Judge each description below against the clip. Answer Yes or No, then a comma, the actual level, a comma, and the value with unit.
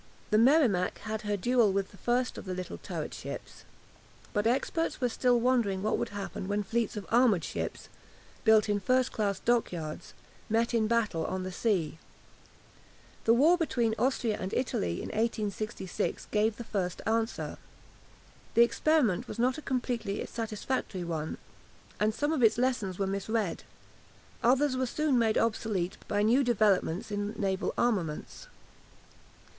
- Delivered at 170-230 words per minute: No, average, 155 wpm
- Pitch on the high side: Yes, high, 220 Hz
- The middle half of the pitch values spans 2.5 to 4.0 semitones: Yes, average, 3.6 semitones